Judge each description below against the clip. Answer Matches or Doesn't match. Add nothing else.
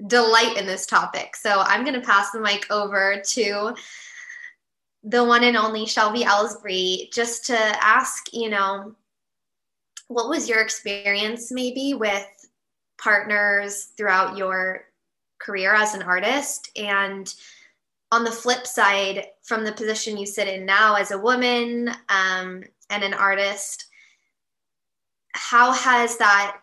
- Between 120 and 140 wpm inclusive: Matches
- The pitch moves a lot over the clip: Doesn't match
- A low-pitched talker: Doesn't match